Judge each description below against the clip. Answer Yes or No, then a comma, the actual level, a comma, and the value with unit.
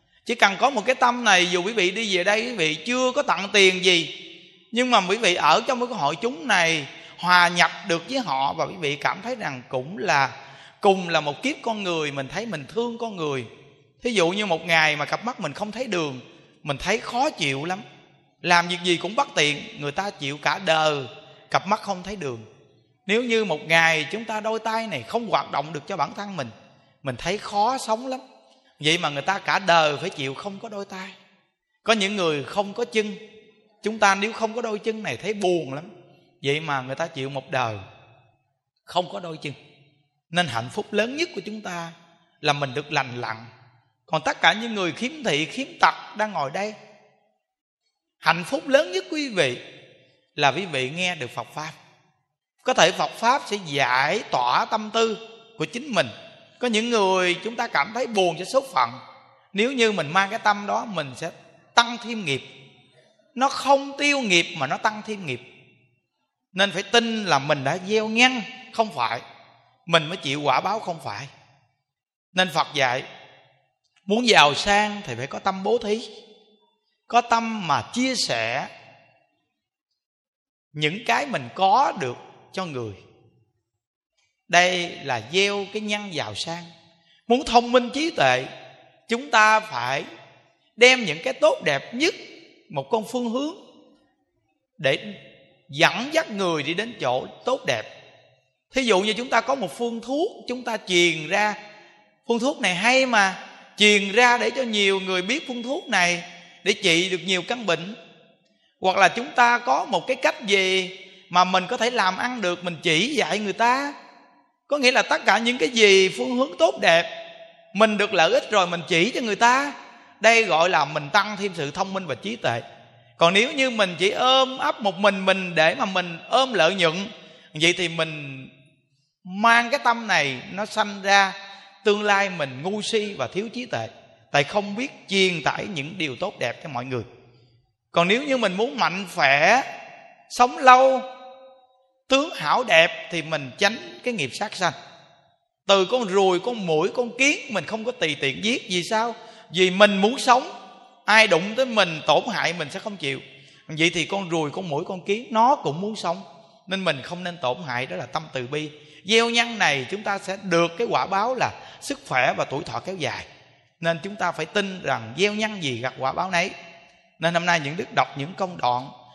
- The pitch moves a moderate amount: No, wide, 6.3 semitones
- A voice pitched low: No, high, 190 Hz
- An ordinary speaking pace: Yes, average, 195 wpm